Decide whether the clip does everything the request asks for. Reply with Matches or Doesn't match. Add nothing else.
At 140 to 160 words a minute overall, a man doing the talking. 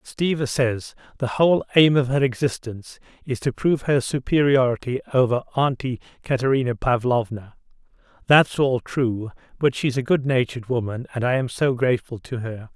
Matches